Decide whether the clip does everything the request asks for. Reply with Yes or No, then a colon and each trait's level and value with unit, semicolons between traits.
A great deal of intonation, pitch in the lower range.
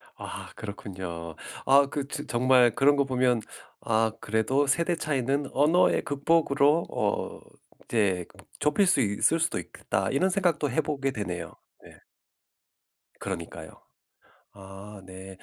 Yes: wide, 6.1 semitones; low, 130 Hz